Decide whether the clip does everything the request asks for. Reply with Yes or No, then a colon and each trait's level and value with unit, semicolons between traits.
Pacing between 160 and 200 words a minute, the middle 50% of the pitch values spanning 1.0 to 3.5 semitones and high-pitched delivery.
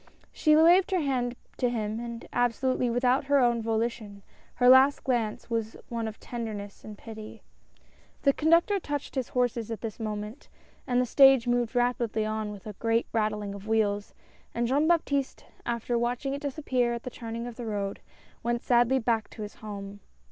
Yes: average, 185 wpm; average, 2.9 semitones; high, 235 Hz